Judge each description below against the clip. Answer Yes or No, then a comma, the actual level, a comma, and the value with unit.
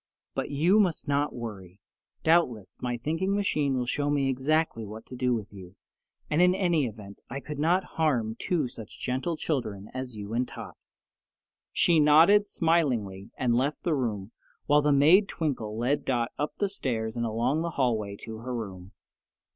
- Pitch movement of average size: No, wide, 5.8 semitones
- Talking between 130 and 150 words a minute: No, average, 175 wpm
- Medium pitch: No, low, 130 Hz